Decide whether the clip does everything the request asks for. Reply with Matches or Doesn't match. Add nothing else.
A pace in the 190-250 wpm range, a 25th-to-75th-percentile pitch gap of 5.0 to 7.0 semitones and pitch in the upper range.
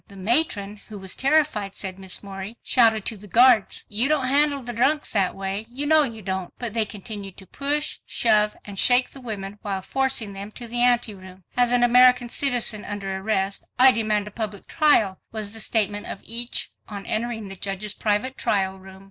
Doesn't match